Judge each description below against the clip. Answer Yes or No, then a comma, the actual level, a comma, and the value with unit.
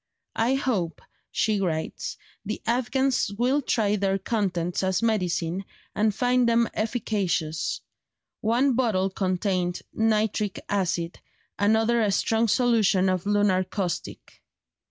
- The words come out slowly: Yes, slow, 115 wpm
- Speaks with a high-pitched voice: Yes, high, 205 Hz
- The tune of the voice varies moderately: Yes, average, 3.7 semitones